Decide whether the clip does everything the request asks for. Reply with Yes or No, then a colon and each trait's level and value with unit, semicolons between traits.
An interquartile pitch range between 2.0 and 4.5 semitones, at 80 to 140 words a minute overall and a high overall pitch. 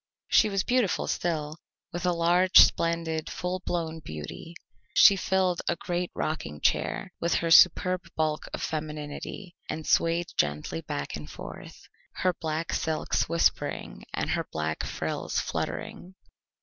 No: narrow, 2.6 semitones; slow, 135 wpm; medium, 165 Hz